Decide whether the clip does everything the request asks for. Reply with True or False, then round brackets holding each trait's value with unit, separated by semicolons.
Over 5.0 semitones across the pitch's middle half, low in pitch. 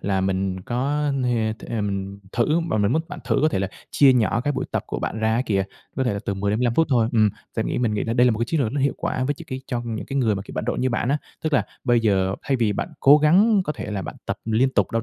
False (4.7 semitones; 120 Hz)